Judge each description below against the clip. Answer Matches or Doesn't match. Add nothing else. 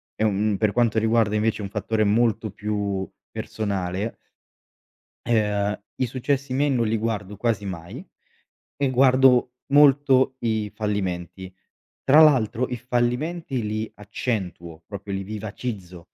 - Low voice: Matches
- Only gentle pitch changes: Doesn't match